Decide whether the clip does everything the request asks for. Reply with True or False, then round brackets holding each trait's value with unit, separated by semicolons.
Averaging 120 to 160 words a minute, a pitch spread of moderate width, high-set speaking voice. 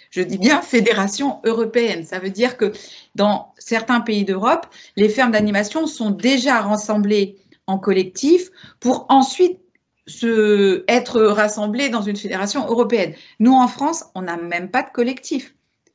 True (145 wpm; 4.3 semitones; 230 Hz)